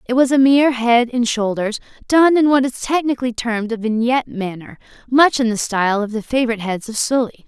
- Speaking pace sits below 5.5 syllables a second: No, 5.9 syllables/s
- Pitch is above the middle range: Yes, high, 240 Hz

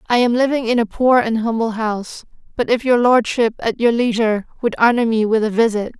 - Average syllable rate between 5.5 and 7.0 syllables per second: Yes, 5.8 syllables/s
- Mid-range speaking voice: No, high, 230 Hz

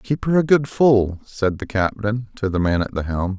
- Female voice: No, male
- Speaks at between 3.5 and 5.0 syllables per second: Yes, 4.6 syllables/s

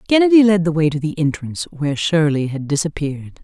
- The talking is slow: No, average, 190 wpm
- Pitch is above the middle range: No, medium, 160 Hz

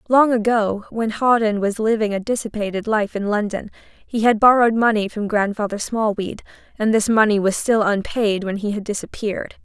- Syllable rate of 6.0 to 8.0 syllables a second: No, 5.3 syllables/s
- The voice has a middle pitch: No, high, 215 Hz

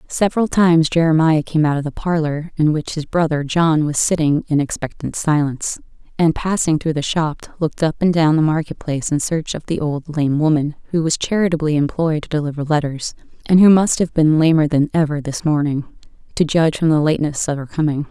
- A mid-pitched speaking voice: Yes, medium, 155 Hz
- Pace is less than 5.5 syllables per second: No, 5.7 syllables/s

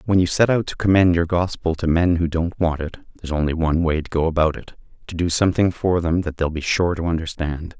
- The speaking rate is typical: No, fast, 245 wpm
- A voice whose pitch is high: No, very low, 85 Hz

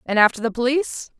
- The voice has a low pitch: No, high, 245 Hz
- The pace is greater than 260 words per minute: No, average, 200 wpm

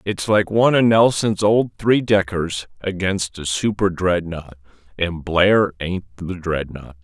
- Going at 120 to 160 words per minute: Yes, average, 145 wpm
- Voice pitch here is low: Yes, very low, 95 Hz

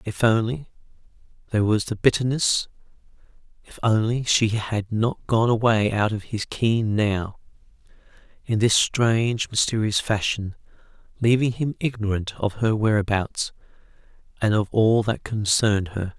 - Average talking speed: No, slow, 120 wpm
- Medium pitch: No, low, 110 Hz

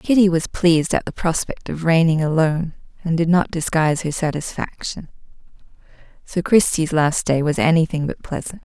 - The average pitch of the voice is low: No, medium, 165 Hz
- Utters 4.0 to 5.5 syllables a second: Yes, 5.3 syllables/s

